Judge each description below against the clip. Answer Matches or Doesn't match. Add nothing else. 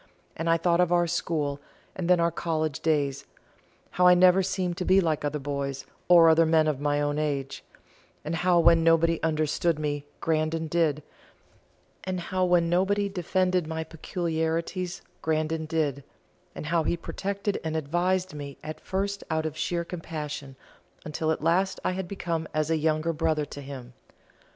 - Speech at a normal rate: Matches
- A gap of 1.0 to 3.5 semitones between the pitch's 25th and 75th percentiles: Matches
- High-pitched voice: Doesn't match